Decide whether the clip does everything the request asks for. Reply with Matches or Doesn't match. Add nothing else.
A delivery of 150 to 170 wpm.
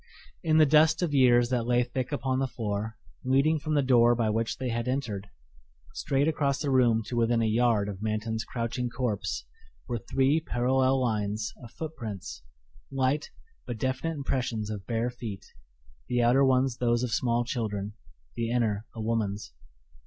Matches